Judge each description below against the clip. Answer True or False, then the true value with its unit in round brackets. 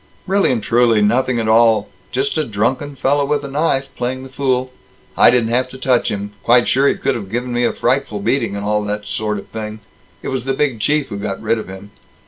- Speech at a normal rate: False (235 wpm)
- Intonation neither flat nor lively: True (3.9 semitones)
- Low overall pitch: True (120 Hz)